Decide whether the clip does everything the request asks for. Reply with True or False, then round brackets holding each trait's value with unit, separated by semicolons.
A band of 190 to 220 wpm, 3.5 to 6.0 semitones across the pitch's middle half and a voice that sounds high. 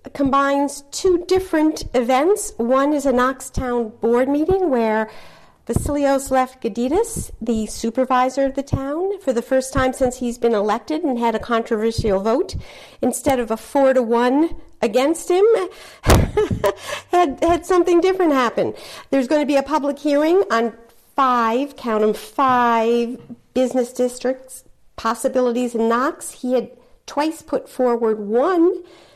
False (140 wpm; 4.0 semitones; 260 Hz)